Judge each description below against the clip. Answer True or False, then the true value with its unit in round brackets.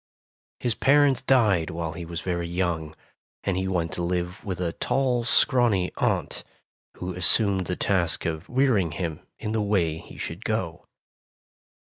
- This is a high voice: False (90 Hz)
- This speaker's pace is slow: False (155 wpm)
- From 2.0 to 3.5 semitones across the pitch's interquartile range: False (4.4 semitones)